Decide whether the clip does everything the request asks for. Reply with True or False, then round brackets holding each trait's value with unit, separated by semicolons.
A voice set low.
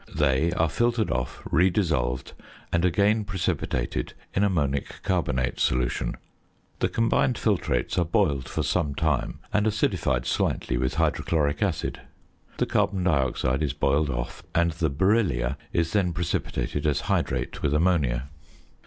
True (80 Hz)